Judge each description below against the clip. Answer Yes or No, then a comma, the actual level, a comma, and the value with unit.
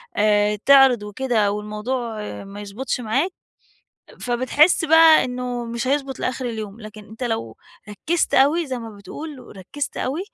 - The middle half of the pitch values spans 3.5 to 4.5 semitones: Yes, average, 4.2 semitones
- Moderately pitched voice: No, high, 245 Hz